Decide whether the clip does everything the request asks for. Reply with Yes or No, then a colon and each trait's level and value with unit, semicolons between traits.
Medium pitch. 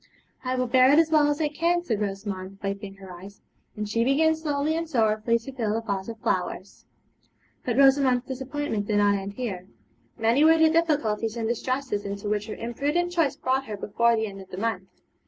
No: high, 235 Hz